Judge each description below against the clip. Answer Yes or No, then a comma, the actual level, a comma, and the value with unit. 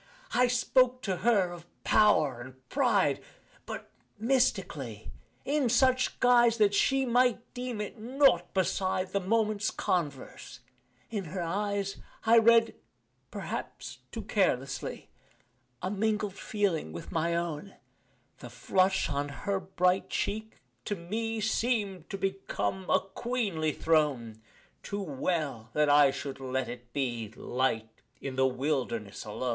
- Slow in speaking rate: Yes, slow, 130 wpm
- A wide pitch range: Yes, wide, 7.5 semitones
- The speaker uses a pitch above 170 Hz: Yes, high, 190 Hz